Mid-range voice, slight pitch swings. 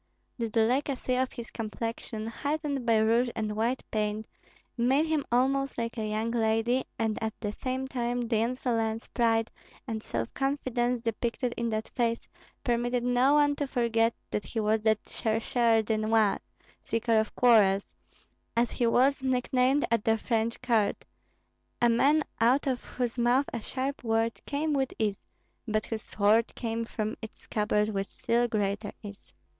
No: high, 230 Hz; narrow, 2.3 semitones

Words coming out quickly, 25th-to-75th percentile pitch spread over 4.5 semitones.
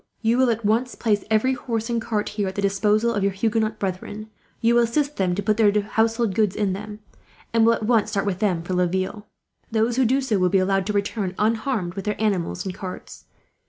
No: fast, 230 wpm; average, 2.7 semitones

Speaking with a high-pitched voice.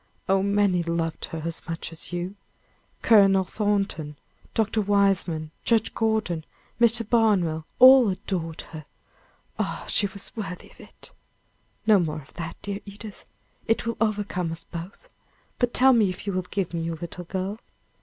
Yes: high, 195 Hz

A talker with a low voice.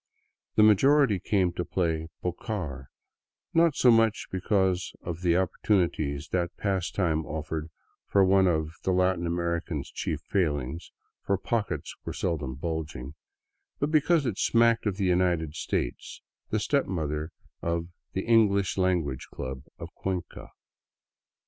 Yes: very low, 90 Hz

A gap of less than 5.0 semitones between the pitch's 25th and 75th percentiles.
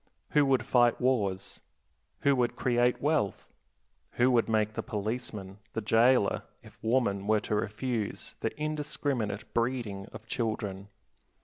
Yes: average, 3.6 semitones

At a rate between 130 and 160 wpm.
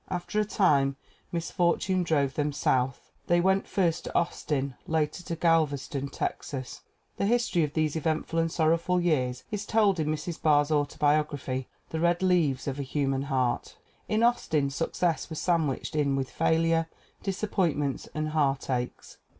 Yes: average, 150 wpm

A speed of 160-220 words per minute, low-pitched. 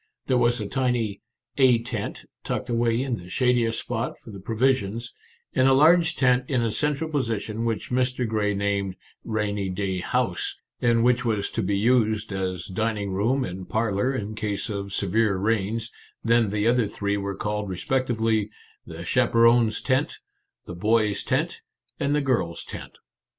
Yes: average, 175 wpm; low, 115 Hz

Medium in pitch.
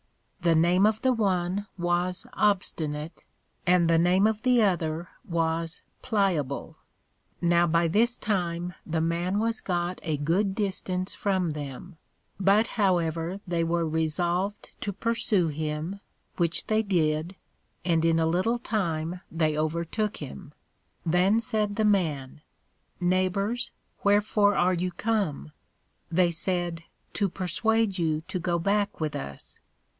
Yes: medium, 180 Hz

